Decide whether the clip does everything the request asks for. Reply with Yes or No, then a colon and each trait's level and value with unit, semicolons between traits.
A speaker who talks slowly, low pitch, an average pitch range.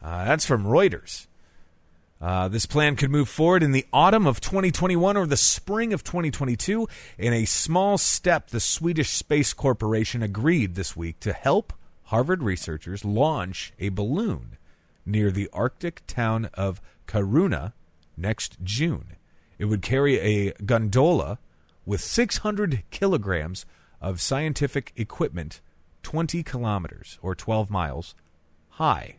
No: slow, 130 wpm; low, 110 Hz; wide, 8.9 semitones